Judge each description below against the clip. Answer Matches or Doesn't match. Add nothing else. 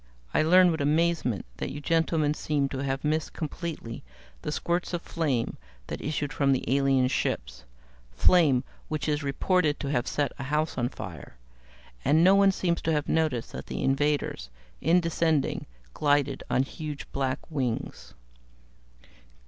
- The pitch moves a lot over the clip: Doesn't match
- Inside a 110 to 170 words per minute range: Matches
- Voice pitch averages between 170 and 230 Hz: Doesn't match